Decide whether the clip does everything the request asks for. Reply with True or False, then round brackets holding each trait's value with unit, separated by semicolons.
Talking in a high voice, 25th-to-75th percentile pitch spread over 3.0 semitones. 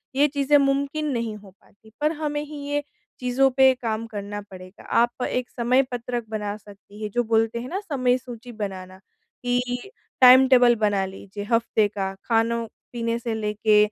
True (235 Hz; 3.5 semitones)